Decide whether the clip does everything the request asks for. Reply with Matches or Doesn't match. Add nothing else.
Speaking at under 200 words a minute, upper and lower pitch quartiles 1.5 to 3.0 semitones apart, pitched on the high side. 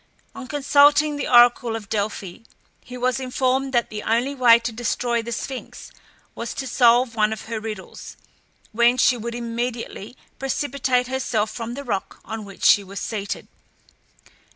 Matches